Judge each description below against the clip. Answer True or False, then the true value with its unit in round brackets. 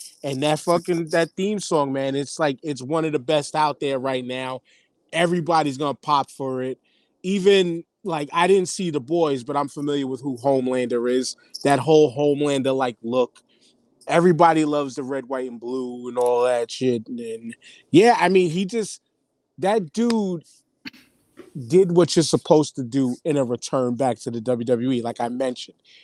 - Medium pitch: True (145 Hz)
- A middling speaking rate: True (180 wpm)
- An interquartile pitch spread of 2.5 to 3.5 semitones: False (4.8 semitones)